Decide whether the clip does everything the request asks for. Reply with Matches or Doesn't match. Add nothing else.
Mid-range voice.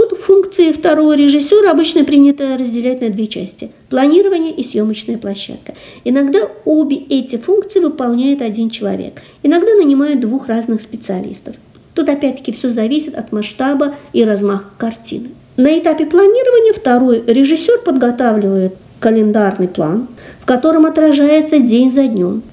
Doesn't match